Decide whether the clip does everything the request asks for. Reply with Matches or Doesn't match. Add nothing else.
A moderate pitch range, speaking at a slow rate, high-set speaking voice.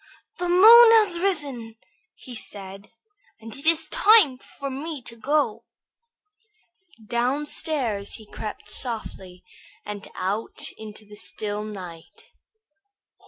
Doesn't match